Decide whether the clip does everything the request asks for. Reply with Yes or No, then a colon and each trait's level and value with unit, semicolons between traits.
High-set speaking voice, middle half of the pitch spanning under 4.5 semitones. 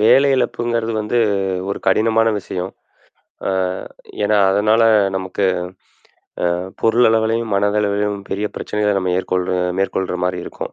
No: low, 105 Hz; average, 2.7 semitones